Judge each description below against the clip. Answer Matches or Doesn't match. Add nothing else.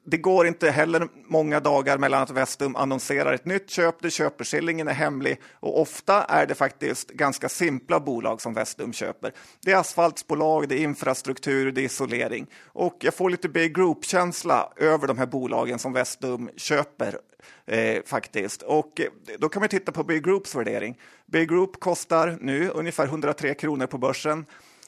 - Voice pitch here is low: Doesn't match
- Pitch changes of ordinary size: Matches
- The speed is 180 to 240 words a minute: Doesn't match